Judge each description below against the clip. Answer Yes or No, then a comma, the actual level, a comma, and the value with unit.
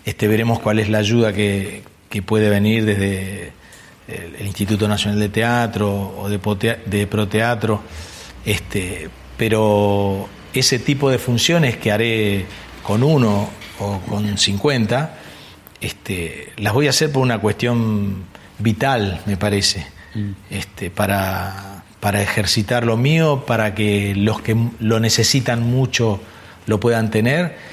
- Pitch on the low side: Yes, low, 105 Hz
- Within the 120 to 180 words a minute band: Yes, average, 130 wpm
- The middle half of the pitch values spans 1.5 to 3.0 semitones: Yes, narrow, 2.4 semitones